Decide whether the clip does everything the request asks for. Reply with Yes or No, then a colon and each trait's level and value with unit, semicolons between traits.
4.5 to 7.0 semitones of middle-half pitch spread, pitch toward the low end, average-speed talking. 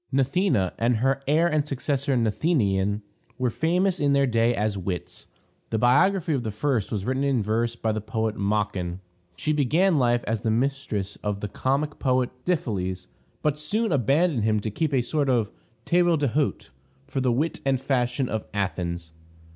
Yes: average, 5.2 semitones; low, 125 Hz; average, 170 wpm